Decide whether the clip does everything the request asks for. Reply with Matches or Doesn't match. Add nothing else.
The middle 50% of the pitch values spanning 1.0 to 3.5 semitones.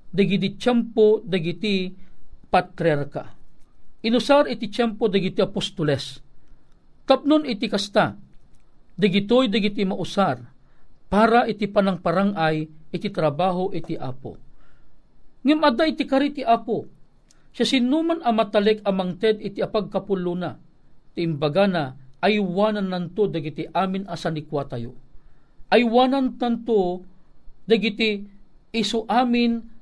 Doesn't match